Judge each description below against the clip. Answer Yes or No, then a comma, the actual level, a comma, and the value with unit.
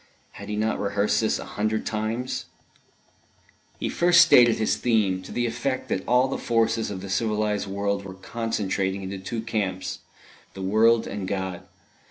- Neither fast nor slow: Yes, average, 165 wpm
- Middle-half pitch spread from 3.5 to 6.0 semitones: No, average, 2.8 semitones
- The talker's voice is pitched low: Yes, low, 105 Hz